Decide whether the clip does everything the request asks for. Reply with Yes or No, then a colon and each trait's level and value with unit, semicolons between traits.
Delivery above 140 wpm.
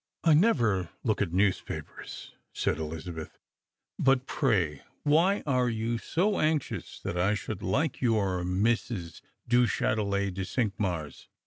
No: slow, 135 wpm